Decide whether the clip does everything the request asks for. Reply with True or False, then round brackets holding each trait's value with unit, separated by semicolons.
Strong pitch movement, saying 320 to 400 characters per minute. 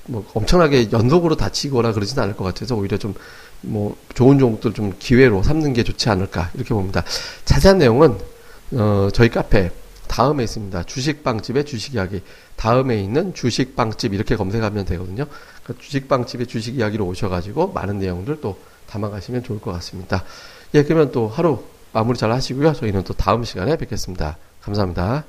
False (4.7 semitones; 390 characters per minute)